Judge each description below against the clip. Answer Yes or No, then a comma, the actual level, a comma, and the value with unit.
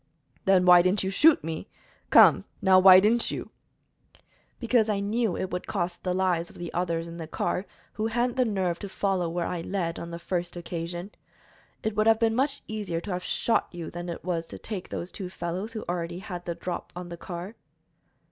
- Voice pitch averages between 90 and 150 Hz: No, medium, 180 Hz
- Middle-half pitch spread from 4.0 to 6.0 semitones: No, average, 3.3 semitones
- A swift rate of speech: Yes, fast, 210 wpm